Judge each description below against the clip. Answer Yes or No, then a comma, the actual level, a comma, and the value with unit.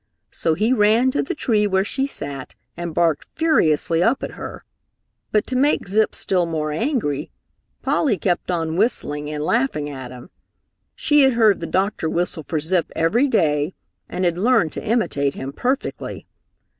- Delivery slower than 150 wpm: No, average, 170 wpm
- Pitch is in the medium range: Yes, medium, 180 Hz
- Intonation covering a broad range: Yes, wide, 7.1 semitones